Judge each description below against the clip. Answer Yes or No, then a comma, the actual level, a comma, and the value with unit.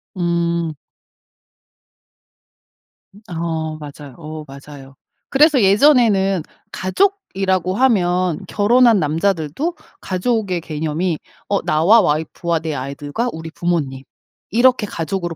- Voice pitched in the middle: Yes, medium, 175 Hz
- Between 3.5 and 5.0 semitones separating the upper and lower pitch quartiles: Yes, average, 4.6 semitones